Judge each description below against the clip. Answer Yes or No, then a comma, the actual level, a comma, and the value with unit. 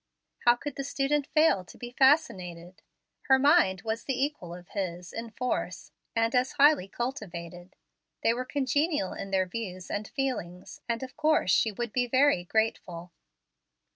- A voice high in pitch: Yes, high, 230 Hz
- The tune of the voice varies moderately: No, wide, 6.7 semitones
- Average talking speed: Yes, average, 160 wpm